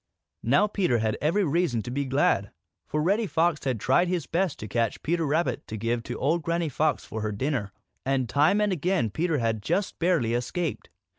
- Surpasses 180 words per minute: Yes, average, 200 wpm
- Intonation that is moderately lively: No, wide, 6.5 semitones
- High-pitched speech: No, medium, 145 Hz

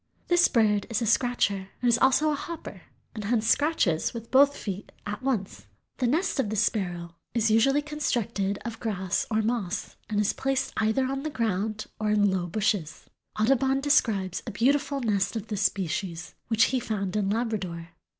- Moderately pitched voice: No, high, 220 Hz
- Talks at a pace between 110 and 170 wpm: No, average, 180 wpm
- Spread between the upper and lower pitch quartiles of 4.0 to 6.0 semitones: Yes, average, 4.5 semitones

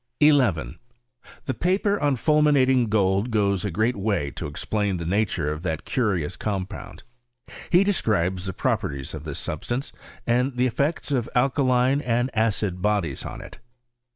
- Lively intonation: Yes, wide, 5.8 semitones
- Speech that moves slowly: No, average, 155 wpm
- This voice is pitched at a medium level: No, low, 110 Hz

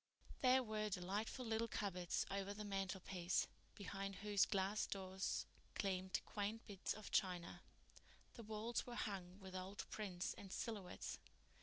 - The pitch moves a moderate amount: No, narrow, 2.3 semitones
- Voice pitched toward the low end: No, high, 200 Hz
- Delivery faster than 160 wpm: No, slow, 135 wpm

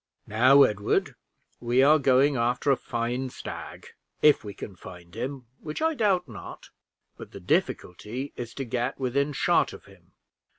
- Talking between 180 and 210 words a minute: No, average, 160 wpm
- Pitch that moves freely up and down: No, average, 3.3 semitones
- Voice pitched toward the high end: No, low, 125 Hz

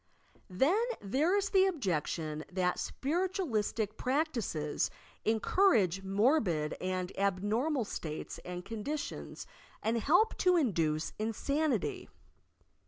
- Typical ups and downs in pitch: No, wide, 9.0 semitones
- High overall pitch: Yes, high, 220 Hz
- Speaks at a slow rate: Yes, slow, 105 wpm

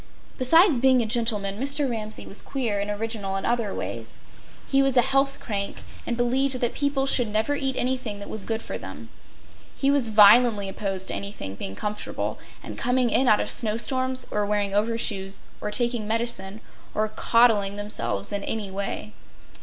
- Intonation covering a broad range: No, average, 3.8 semitones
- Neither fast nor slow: Yes, average, 175 wpm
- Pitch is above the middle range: Yes, high, 225 Hz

